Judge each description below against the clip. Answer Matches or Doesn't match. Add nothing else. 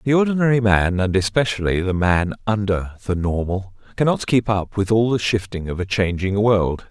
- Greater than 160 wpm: Matches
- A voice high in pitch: Doesn't match